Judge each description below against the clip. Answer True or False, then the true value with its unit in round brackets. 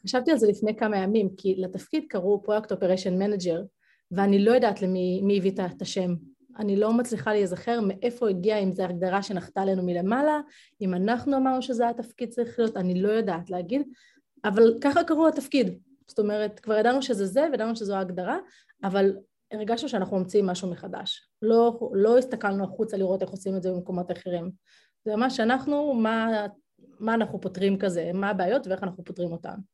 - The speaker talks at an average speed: False (175 wpm)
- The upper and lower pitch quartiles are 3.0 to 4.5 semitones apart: True (4.0 semitones)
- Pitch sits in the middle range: False (205 Hz)